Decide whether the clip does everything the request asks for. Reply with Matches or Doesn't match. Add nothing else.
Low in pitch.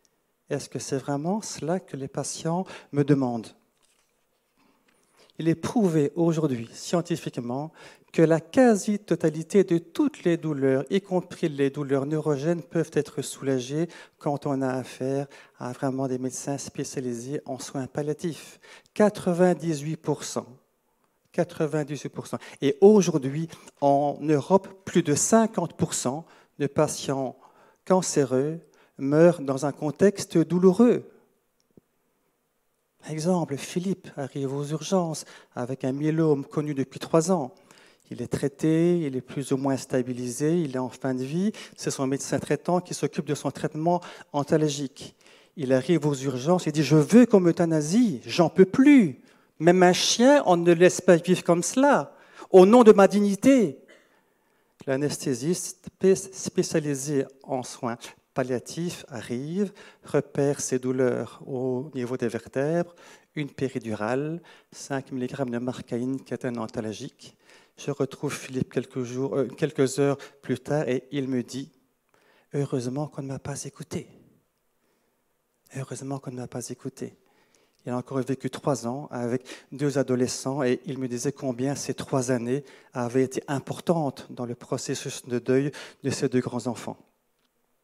Doesn't match